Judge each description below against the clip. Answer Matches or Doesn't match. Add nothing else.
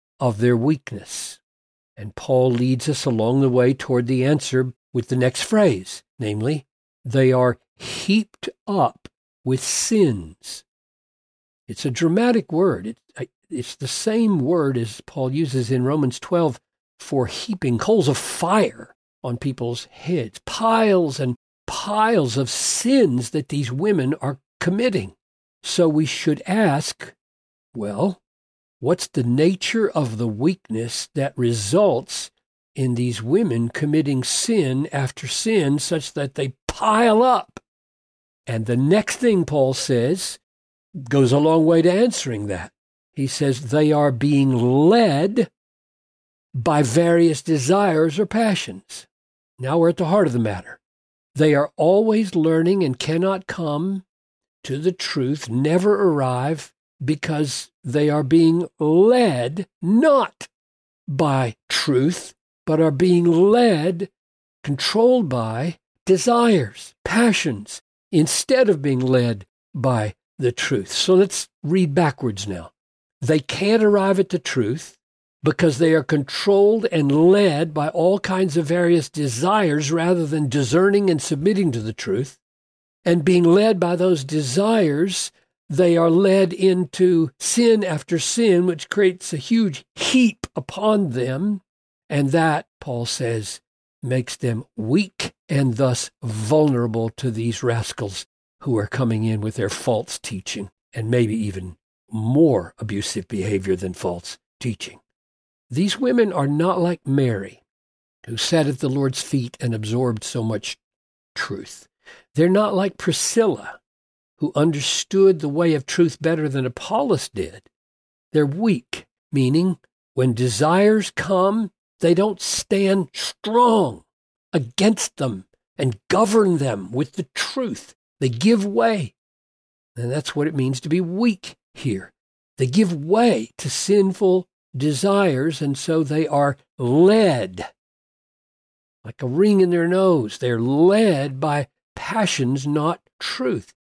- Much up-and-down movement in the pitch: Matches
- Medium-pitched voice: Matches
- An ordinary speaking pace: Doesn't match